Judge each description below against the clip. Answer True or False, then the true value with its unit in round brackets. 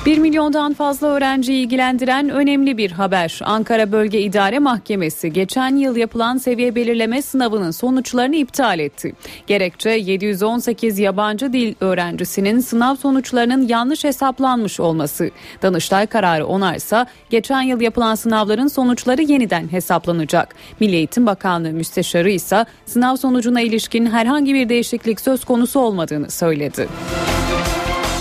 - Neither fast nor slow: True (120 wpm)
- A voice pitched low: False (230 Hz)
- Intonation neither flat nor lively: True (4.9 semitones)